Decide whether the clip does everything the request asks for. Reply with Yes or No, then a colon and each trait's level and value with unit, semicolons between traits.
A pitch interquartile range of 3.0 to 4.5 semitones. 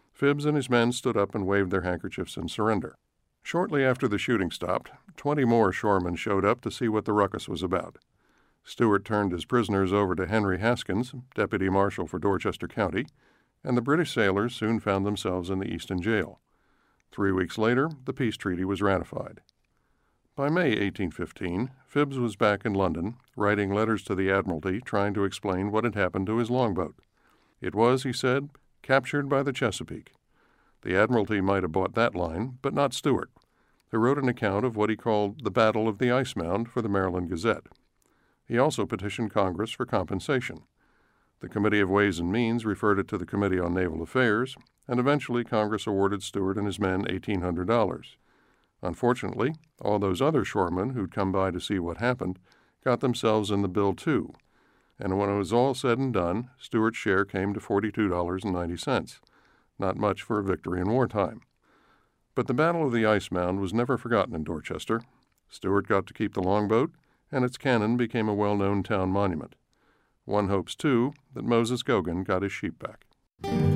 Yes: average, 4.0 semitones